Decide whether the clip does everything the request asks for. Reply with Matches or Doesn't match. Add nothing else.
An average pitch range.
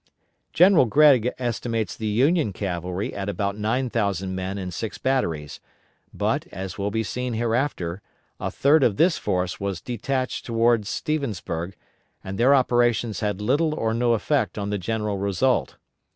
Matches